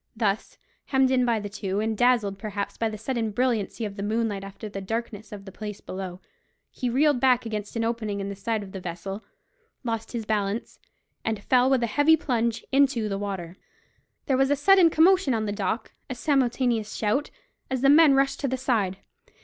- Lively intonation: No, average, 4.2 semitones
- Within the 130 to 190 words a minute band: No, average, 200 wpm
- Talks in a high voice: Yes, high, 225 Hz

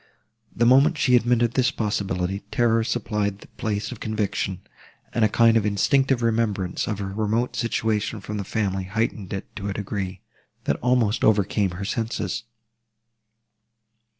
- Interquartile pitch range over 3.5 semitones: No, average, 2.7 semitones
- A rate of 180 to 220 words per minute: No, average, 150 wpm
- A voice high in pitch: No, low, 110 Hz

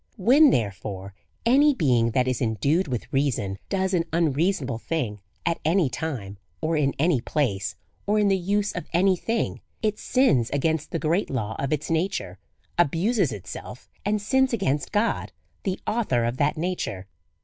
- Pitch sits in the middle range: Yes, medium, 155 Hz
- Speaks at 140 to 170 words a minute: Yes, average, 160 wpm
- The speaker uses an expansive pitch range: Yes, wide, 8.0 semitones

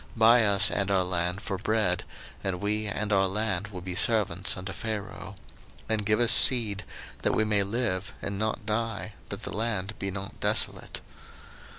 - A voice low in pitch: Yes, low, 100 Hz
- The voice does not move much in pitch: Yes, narrow, 2.2 semitones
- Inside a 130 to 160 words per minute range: No, average, 175 wpm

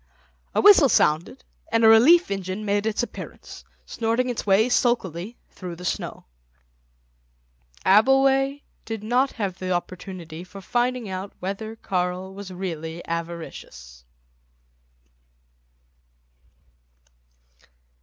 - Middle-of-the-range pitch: No, high, 200 Hz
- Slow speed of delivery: Yes, slow, 105 wpm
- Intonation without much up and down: No, average, 5.0 semitones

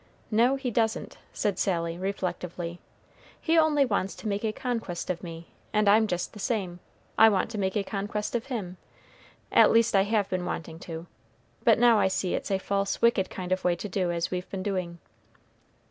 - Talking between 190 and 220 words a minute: Yes, average, 195 wpm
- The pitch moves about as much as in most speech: Yes, average, 3.7 semitones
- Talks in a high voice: Yes, high, 195 Hz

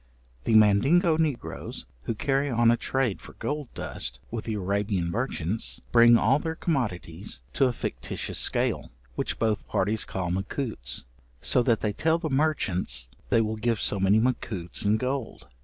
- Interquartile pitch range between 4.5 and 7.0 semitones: Yes, average, 5.2 semitones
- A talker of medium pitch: No, low, 110 Hz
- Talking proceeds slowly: No, average, 160 wpm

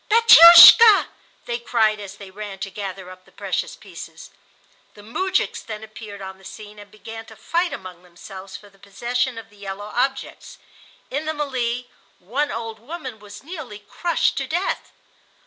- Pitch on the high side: Yes, high, 220 Hz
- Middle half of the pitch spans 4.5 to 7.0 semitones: Yes, average, 5.1 semitones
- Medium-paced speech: Yes, average, 165 wpm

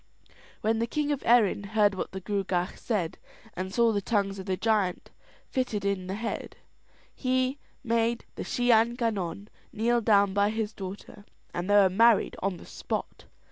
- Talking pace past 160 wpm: Yes, average, 175 wpm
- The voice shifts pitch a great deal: No, average, 3.1 semitones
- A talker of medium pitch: No, high, 210 Hz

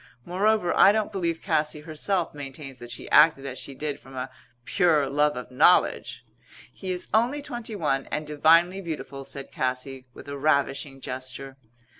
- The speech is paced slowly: No, average, 165 wpm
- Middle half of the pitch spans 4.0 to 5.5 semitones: Yes, average, 4.7 semitones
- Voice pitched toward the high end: No, medium, 150 Hz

